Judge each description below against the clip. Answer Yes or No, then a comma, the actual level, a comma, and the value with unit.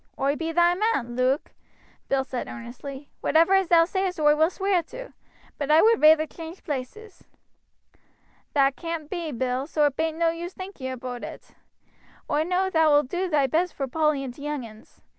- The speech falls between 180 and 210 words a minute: Yes, average, 185 wpm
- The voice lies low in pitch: No, very high, 310 Hz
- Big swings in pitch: No, average, 4.2 semitones